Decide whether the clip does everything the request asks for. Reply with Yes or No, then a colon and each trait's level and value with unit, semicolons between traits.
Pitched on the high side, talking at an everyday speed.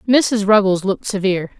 Yes: high, 200 Hz; average, 150 wpm